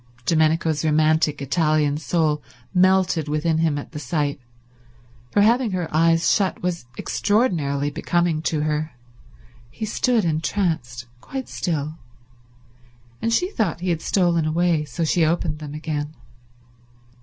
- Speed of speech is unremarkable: No, slow, 130 wpm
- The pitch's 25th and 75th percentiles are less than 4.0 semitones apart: Yes, average, 2.8 semitones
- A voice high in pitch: No, medium, 160 Hz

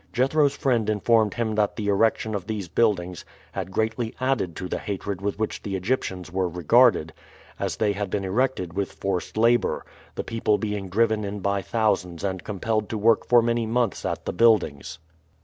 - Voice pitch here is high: No, low, 105 Hz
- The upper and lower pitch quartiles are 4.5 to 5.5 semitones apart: No, average, 3.2 semitones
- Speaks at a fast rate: No, average, 185 wpm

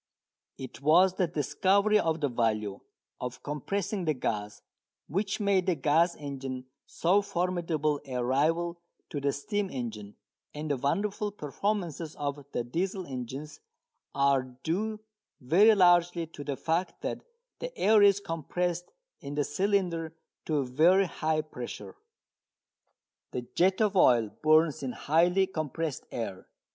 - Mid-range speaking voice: Yes, medium, 160 Hz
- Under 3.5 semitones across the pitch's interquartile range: No, average, 5.3 semitones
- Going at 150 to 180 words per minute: No, slow, 135 wpm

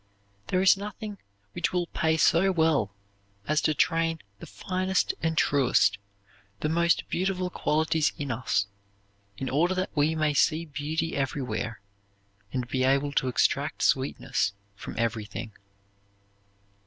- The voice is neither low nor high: Yes, medium, 155 Hz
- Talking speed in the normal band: No, slow, 130 wpm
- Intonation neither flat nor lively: Yes, average, 4.5 semitones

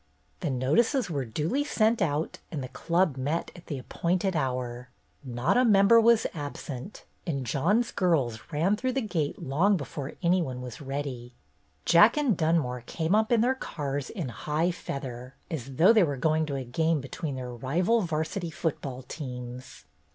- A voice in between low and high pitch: Yes, medium, 155 Hz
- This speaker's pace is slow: No, average, 170 wpm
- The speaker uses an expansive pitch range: Yes, wide, 6.1 semitones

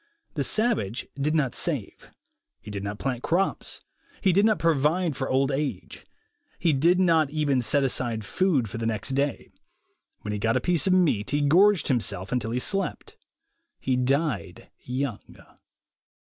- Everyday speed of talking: Yes, average, 165 wpm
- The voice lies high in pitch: No, medium, 140 Hz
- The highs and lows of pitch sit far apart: Yes, wide, 5.9 semitones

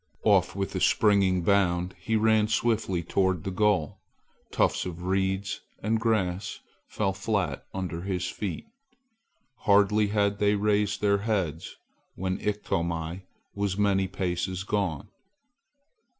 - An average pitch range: No, narrow, 2.3 semitones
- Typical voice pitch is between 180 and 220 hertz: No, very low, 95 Hz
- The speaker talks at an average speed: No, slow, 120 wpm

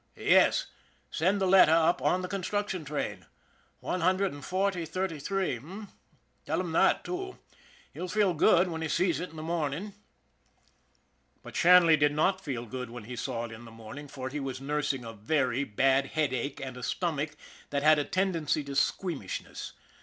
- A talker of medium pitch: Yes, medium, 155 Hz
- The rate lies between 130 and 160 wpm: No, average, 180 wpm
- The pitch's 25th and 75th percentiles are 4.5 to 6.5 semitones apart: Yes, average, 5.3 semitones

